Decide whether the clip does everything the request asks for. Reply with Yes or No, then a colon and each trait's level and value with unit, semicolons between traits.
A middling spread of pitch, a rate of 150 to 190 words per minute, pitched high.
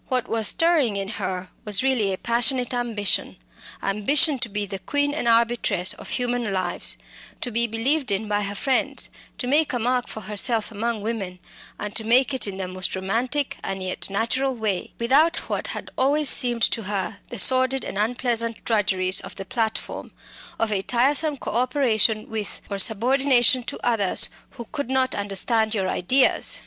Yes: average, 4.1 semitones; average, 175 wpm; high, 230 Hz